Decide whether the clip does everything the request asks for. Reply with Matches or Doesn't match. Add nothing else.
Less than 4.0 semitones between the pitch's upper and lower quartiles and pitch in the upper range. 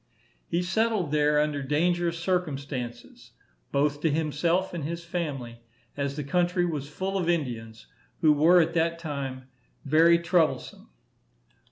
Doesn't match